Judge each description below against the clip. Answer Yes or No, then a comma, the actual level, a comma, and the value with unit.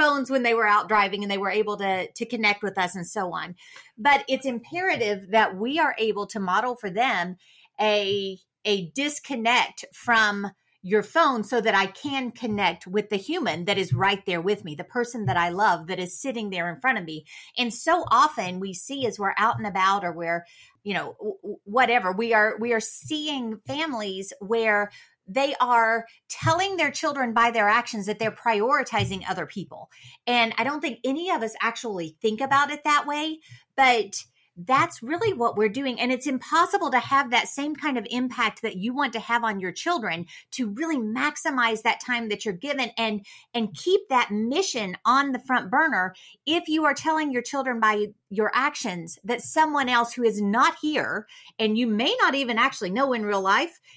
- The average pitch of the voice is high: Yes, high, 230 Hz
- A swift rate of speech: No, average, 195 wpm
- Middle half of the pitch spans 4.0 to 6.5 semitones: Yes, average, 5.2 semitones